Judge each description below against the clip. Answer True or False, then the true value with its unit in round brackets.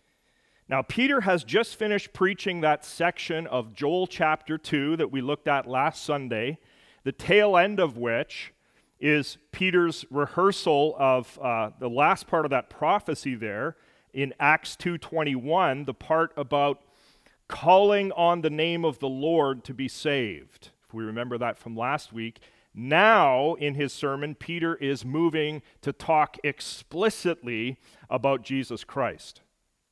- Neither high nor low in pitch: True (145 Hz)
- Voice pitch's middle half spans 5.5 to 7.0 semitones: False (3.9 semitones)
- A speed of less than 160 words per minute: True (140 wpm)